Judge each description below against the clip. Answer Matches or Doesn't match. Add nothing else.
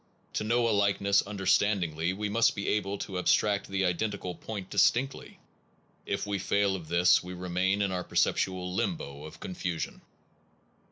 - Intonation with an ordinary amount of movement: Doesn't match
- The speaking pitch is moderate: Doesn't match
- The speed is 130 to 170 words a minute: Matches